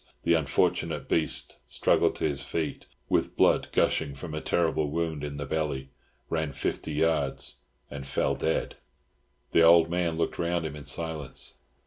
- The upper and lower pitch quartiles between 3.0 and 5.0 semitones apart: No, narrow, 2.4 semitones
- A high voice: No, very low, 80 Hz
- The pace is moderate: Yes, average, 155 wpm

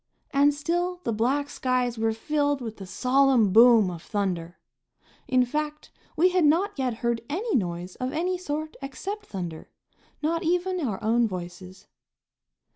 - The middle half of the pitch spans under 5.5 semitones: No, wide, 6.0 semitones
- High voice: Yes, very high, 255 Hz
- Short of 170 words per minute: Yes, average, 150 wpm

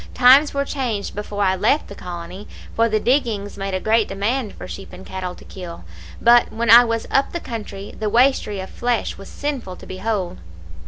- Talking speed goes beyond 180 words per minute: Yes, average, 200 wpm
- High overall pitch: Yes, high, 215 Hz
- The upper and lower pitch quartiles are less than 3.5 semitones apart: No, average, 3.9 semitones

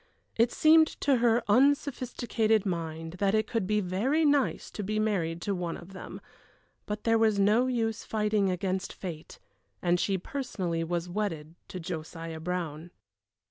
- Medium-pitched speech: No, high, 200 Hz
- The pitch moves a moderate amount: Yes, average, 4.5 semitones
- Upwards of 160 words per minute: No, average, 155 wpm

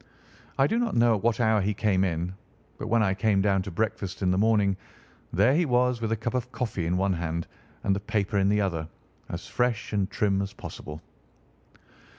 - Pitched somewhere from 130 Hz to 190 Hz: No, low, 105 Hz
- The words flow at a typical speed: No, fast, 210 wpm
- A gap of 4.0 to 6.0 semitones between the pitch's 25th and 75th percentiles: No, average, 3.2 semitones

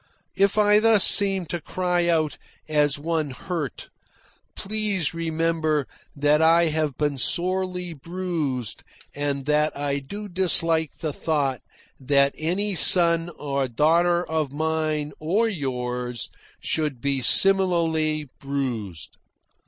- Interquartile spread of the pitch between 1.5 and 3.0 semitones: No, average, 3.7 semitones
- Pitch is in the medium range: Yes, medium, 160 Hz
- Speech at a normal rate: No, slow, 115 wpm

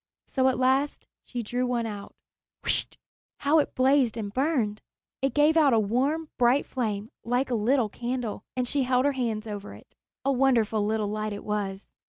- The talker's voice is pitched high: Yes, high, 245 Hz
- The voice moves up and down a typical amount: Yes, average, 3.9 semitones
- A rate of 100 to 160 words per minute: No, average, 185 wpm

